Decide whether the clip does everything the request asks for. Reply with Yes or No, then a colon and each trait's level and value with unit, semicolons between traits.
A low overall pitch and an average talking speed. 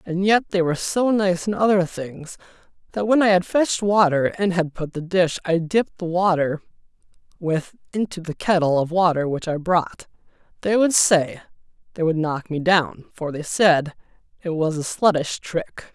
No: medium, 175 Hz; average, 185 wpm